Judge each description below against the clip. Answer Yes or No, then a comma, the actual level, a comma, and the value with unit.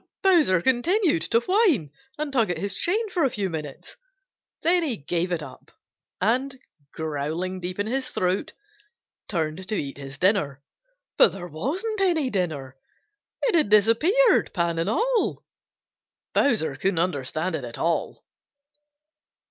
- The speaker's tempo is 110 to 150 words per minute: Yes, average, 140 wpm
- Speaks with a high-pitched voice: Yes, high, 195 Hz